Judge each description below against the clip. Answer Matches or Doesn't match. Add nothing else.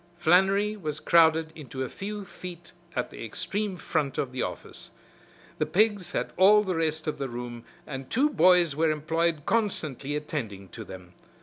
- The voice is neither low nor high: Matches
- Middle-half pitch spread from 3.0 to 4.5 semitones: Doesn't match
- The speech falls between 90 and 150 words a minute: Doesn't match